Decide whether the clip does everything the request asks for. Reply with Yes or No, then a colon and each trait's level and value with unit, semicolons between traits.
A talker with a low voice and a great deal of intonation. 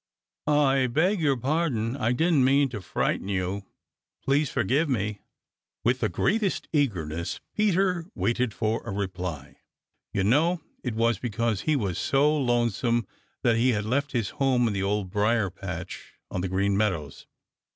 Yes: low, 120 Hz; wide, 5.9 semitones